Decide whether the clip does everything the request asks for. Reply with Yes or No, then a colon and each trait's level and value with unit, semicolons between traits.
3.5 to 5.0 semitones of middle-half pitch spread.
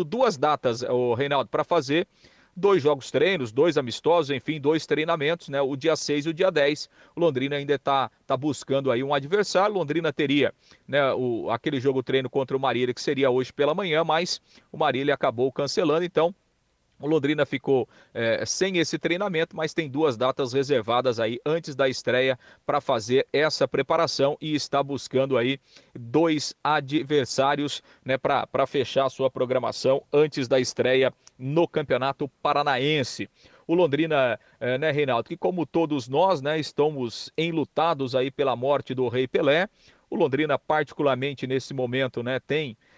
No: average, 2.9 semitones